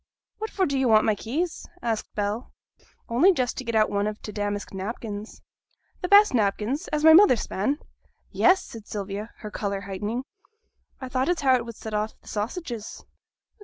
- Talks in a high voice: Yes, high, 225 Hz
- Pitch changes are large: No, average, 4.7 semitones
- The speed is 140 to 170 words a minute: No, average, 185 wpm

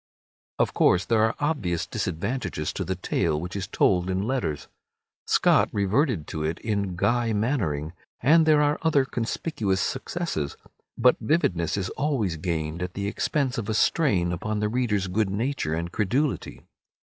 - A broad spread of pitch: Yes, wide, 6.5 semitones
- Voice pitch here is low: Yes, low, 105 Hz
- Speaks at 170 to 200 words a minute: No, average, 160 wpm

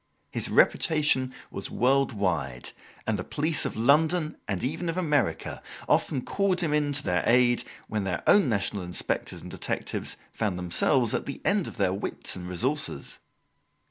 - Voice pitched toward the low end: Yes, low, 130 Hz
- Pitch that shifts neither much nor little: No, wide, 7.8 semitones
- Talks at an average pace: Yes, average, 165 wpm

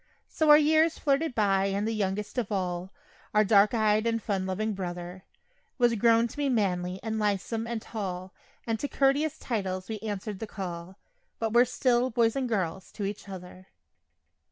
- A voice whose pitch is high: Yes, high, 215 Hz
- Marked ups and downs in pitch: No, average, 3.7 semitones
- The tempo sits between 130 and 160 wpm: No, average, 180 wpm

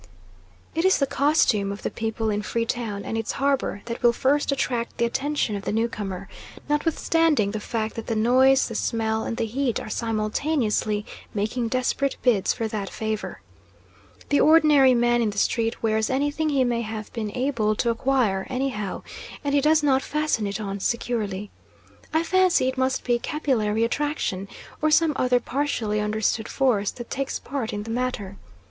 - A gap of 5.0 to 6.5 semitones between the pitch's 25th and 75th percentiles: No, average, 4.2 semitones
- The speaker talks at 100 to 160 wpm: No, average, 175 wpm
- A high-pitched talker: Yes, high, 235 Hz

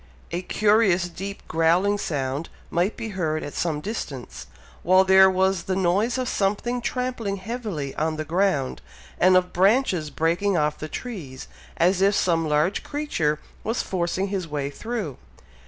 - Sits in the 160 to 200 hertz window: Yes, medium, 185 Hz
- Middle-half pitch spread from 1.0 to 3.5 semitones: No, average, 4.3 semitones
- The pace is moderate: Yes, average, 155 wpm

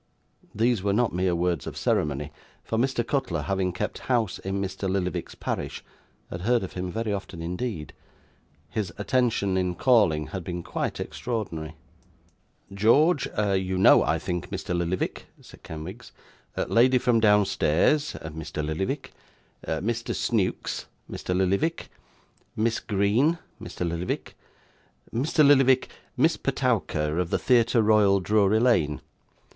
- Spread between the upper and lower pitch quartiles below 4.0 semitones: No, average, 4.9 semitones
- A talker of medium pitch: No, low, 100 Hz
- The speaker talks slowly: Yes, slow, 130 wpm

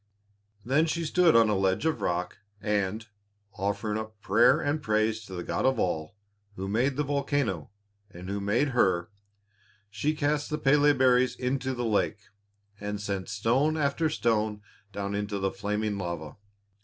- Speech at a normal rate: Yes, average, 160 wpm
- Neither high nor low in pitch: No, low, 110 Hz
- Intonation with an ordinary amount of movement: No, wide, 5.7 semitones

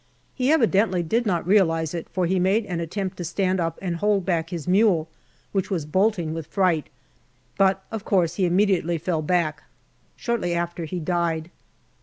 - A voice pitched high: No, medium, 180 Hz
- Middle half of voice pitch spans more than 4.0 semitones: No, average, 2.8 semitones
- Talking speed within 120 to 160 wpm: No, average, 175 wpm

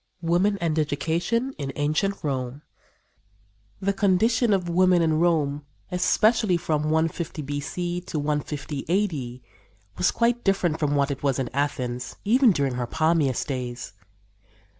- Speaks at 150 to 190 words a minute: No, slow, 135 wpm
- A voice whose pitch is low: No, medium, 160 Hz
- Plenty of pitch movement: No, average, 4.5 semitones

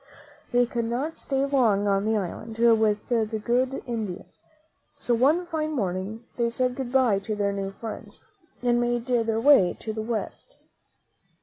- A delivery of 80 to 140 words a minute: No, average, 165 wpm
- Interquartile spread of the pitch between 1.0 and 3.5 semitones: Yes, average, 3.0 semitones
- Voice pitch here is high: Yes, high, 235 Hz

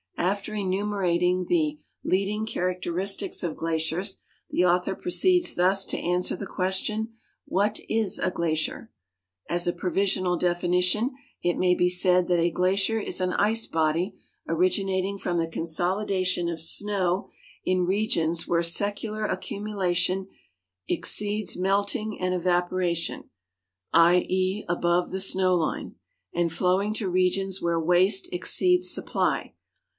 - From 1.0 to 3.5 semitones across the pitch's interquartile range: Yes, narrow, 2.5 semitones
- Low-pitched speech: No, medium, 185 Hz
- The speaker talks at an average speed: No, slow, 130 wpm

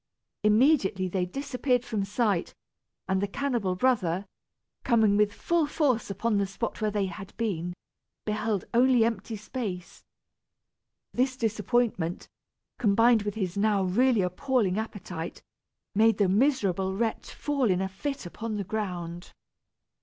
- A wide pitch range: No, average, 3.9 semitones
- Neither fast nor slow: No, slow, 130 wpm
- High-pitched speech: Yes, high, 210 Hz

